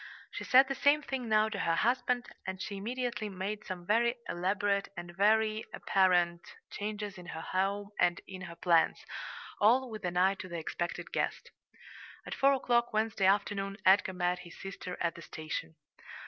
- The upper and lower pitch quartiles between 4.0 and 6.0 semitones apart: No, average, 3.6 semitones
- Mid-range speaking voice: No, high, 200 Hz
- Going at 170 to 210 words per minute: Yes, average, 175 wpm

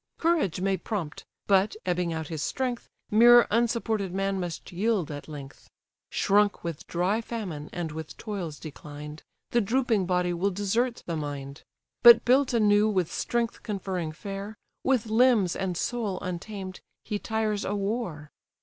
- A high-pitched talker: Yes, high, 195 Hz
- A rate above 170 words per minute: No, average, 150 wpm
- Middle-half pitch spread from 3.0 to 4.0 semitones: No, average, 4.7 semitones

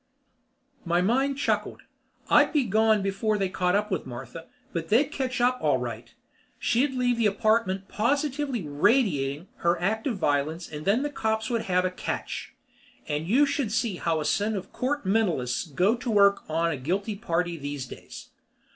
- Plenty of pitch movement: Yes, wide, 5.8 semitones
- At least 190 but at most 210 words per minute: No, average, 175 wpm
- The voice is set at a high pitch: Yes, high, 200 Hz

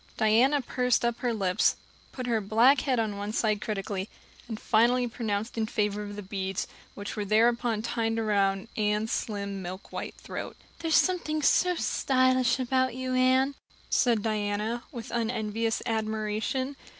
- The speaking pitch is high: Yes, high, 225 Hz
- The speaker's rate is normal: Yes, average, 150 wpm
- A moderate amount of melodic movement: Yes, average, 3.2 semitones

